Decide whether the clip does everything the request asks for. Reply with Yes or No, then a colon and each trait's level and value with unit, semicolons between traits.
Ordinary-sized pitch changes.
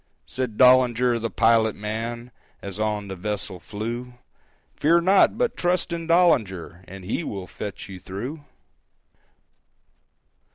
Yes: average, 4.3 semitones